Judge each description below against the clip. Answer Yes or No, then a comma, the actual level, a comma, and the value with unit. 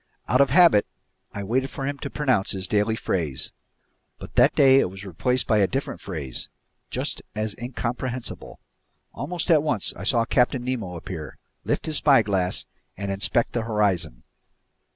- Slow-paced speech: No, average, 160 wpm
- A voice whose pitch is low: Yes, low, 115 Hz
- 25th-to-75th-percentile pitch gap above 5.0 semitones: Yes, wide, 5.4 semitones